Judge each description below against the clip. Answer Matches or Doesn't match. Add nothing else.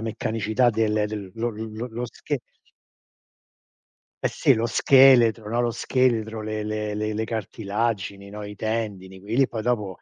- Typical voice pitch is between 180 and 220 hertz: Doesn't match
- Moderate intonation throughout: Doesn't match